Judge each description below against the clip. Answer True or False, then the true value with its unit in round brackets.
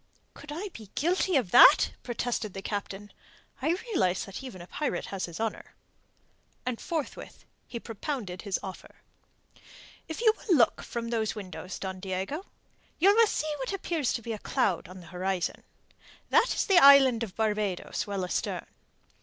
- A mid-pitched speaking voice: False (225 Hz)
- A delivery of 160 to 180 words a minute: True (165 wpm)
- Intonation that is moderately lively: False (7.6 semitones)